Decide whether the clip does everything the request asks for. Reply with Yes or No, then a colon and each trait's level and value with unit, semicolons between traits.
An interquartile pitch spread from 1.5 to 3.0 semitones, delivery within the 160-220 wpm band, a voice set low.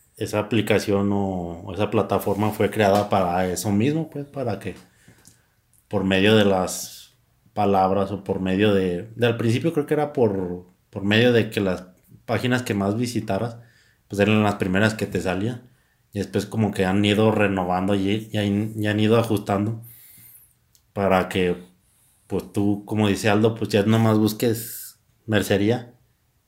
Yes: narrow, 2.5 semitones; average, 165 wpm; low, 105 Hz